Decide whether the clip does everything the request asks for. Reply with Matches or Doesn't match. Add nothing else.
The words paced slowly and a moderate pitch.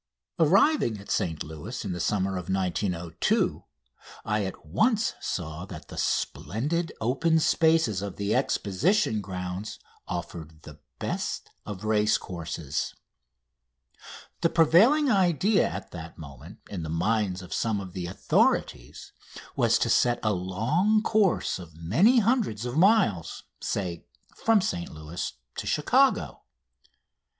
Doesn't match